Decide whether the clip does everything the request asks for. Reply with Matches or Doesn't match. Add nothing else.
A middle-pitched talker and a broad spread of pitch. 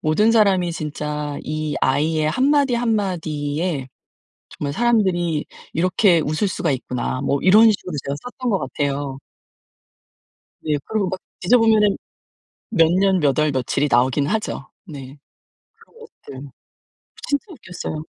Matches